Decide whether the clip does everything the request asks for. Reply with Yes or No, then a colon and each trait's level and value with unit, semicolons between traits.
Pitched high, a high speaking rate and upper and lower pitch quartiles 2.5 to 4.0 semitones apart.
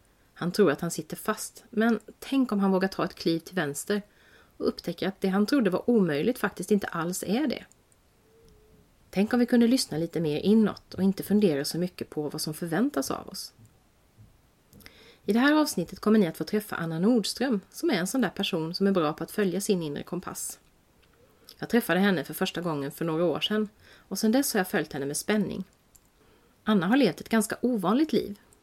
No: high, 195 Hz; fast, 210 wpm; average, 4.6 semitones